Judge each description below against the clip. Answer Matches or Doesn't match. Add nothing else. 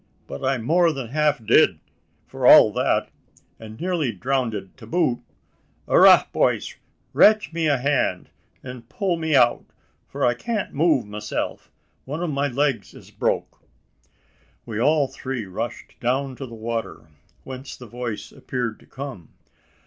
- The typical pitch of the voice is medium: Doesn't match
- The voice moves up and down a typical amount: Matches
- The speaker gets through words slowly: Doesn't match